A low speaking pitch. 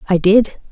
No: high, 200 Hz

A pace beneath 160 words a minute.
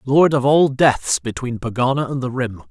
No: average, 200 wpm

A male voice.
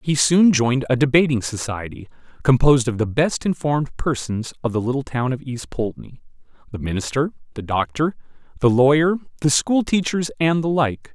Yes: male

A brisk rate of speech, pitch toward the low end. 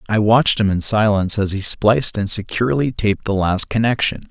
No: average, 195 wpm; low, 105 Hz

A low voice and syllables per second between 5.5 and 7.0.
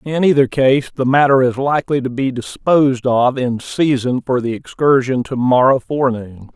No: low, 130 Hz; 4.9 syllables/s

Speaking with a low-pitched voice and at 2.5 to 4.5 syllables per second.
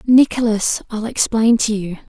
No: high, 220 Hz; 4.4 syllables/s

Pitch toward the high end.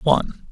No: medium, 150 Hz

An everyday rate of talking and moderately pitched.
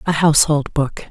Yes: average, 165 wpm; medium, 150 Hz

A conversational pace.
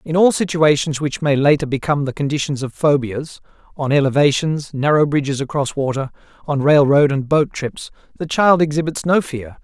Yes: average, 170 wpm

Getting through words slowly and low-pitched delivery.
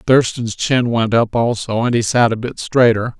No: fast, 205 wpm; low, 115 Hz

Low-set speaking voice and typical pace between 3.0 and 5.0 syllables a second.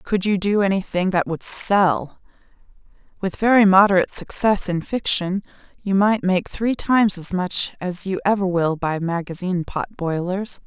No: high, 190 Hz; 4.6 syllables/s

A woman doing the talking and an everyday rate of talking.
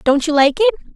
No: female; fast, 255 wpm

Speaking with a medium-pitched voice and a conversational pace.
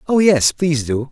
No: medium, 150 Hz; fast, 215 wpm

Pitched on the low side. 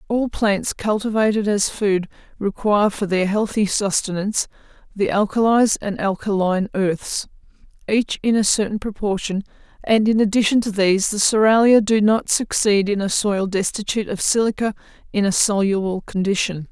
No: high, 205 Hz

